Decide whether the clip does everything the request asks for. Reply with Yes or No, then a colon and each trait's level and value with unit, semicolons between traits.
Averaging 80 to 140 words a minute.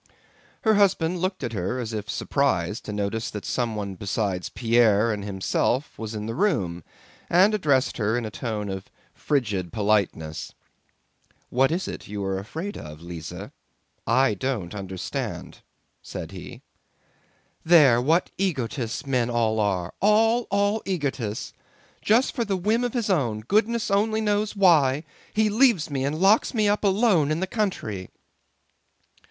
No: average, 150 wpm